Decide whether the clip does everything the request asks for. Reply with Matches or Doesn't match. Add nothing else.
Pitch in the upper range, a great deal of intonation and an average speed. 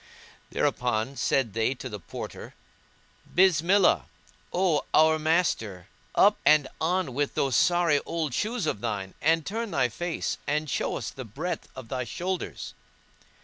Doesn't match